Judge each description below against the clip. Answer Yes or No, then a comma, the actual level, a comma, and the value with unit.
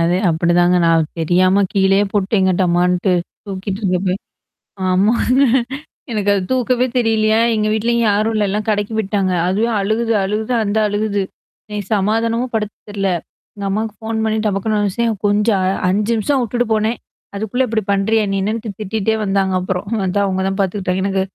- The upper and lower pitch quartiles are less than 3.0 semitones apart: Yes, narrow, 2.4 semitones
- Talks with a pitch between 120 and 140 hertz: No, high, 205 Hz